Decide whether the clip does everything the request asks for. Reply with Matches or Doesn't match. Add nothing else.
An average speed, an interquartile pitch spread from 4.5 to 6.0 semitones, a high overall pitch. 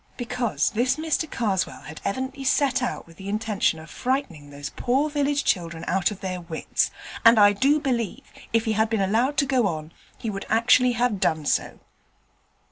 Matches